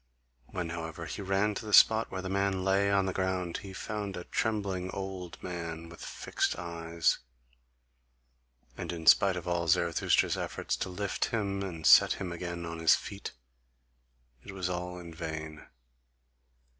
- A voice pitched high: No, very low, 90 Hz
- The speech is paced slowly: No, average, 160 wpm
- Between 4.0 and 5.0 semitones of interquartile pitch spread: No, narrow, 2.6 semitones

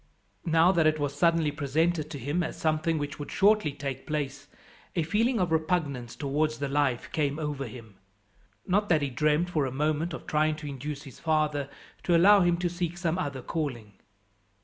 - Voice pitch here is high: No, medium, 155 Hz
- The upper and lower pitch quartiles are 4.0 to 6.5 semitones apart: No, average, 2.9 semitones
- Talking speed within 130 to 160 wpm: No, average, 190 wpm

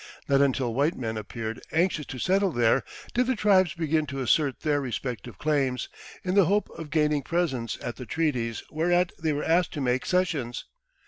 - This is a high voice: No, medium, 150 Hz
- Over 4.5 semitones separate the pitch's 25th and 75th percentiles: Yes, average, 5.2 semitones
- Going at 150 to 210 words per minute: Yes, average, 185 wpm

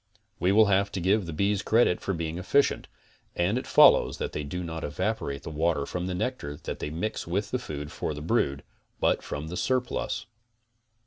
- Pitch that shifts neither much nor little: Yes, average, 4.9 semitones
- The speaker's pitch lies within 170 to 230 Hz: No, very low, 90 Hz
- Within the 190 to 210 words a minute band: Yes, average, 200 wpm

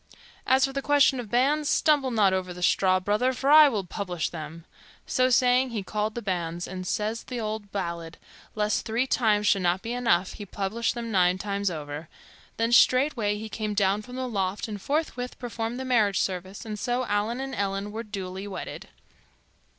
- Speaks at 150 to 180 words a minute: No, average, 190 wpm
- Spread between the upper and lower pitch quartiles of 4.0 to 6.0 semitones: Yes, average, 4.5 semitones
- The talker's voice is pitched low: No, high, 210 Hz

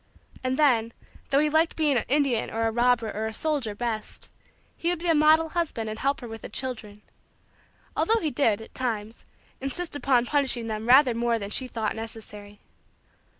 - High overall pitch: Yes, high, 245 Hz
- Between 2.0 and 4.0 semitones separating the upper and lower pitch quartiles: No, average, 4.6 semitones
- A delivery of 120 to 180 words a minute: No, average, 190 wpm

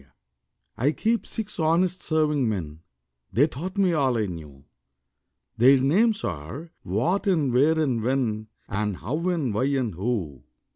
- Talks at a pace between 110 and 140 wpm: No, average, 150 wpm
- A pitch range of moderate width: No, wide, 7.2 semitones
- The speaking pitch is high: No, low, 130 Hz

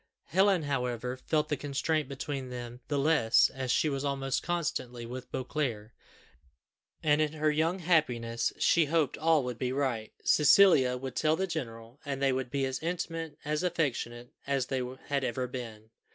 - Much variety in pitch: No, average, 3.7 semitones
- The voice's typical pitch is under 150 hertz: Yes, low, 135 Hz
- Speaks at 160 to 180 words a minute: Yes, average, 165 wpm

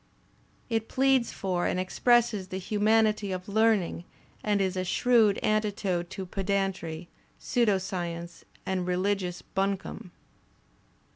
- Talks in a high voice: Yes, high, 195 Hz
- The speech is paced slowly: Yes, slow, 115 wpm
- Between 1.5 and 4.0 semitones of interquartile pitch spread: Yes, average, 2.8 semitones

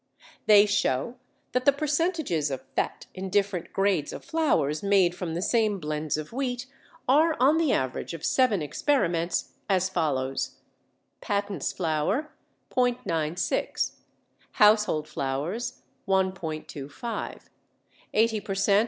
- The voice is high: Yes, high, 195 Hz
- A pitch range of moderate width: No, wide, 7.3 semitones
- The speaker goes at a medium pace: No, slow, 120 wpm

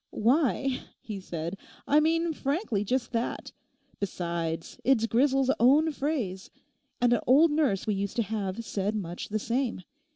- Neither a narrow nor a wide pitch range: No, wide, 5.7 semitones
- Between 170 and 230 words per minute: No, average, 150 wpm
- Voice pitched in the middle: No, high, 230 Hz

